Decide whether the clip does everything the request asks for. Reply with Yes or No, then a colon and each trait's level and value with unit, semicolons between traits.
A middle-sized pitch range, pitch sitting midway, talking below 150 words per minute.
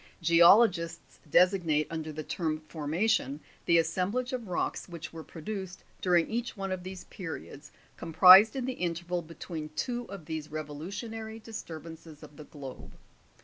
No: average, 3.8 semitones; medium, 170 Hz; average, 155 wpm